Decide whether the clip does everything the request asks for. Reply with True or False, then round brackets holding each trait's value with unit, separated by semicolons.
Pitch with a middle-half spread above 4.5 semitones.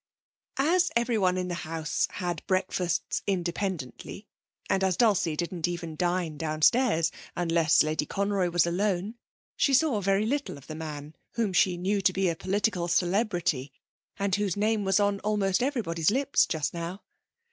False (3.5 semitones)